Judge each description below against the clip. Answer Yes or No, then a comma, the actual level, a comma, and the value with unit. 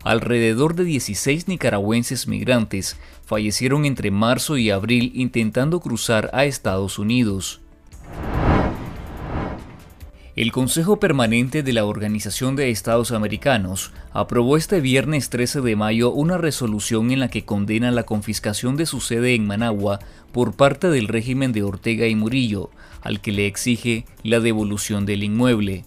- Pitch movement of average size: Yes, average, 3.6 semitones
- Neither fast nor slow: Yes, average, 135 wpm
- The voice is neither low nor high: No, low, 115 Hz